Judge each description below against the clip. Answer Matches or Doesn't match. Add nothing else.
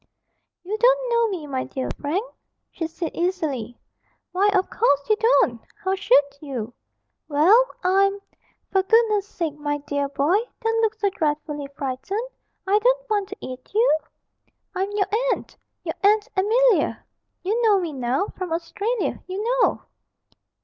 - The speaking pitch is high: Matches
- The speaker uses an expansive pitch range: Matches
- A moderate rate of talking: Matches